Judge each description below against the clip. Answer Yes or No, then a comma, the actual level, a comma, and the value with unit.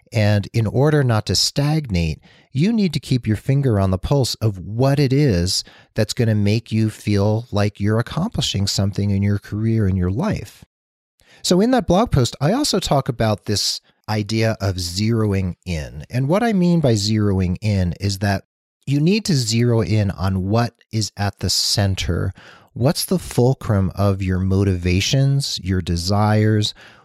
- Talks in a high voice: No, low, 105 Hz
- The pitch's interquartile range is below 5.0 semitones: No, average, 5.3 semitones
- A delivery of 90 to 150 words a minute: No, average, 170 wpm